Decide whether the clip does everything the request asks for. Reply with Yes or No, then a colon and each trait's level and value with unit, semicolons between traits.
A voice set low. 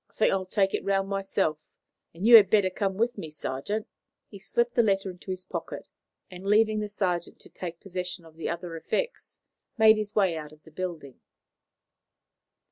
No: high, 190 Hz